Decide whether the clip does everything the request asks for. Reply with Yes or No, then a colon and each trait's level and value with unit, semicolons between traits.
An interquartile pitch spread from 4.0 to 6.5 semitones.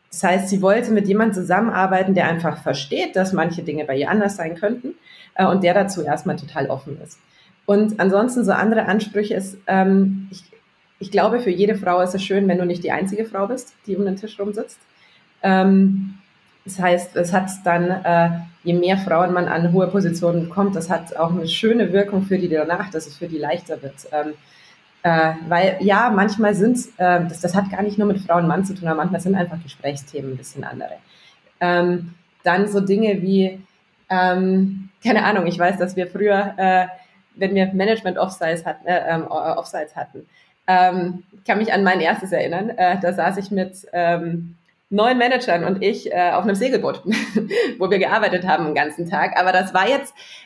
No: narrow, 2.6 semitones